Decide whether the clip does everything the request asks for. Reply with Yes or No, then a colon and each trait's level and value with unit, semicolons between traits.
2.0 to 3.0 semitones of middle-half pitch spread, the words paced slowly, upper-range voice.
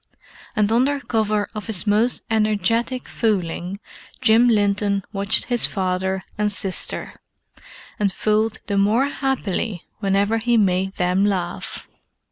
Yes: average, 2.7 semitones; slow, 120 wpm; high, 210 Hz